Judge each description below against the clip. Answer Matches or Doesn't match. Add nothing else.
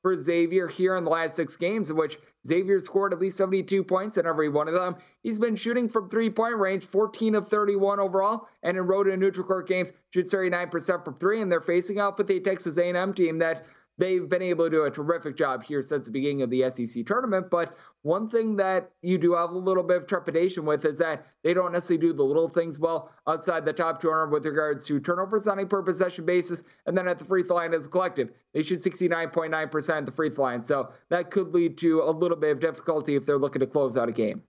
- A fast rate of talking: Matches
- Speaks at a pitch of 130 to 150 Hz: Doesn't match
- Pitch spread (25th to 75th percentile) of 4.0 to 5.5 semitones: Doesn't match